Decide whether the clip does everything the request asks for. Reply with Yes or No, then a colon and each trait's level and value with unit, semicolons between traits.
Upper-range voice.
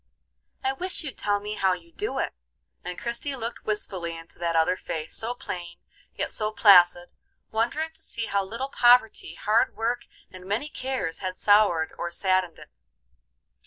Yes: high, 205 Hz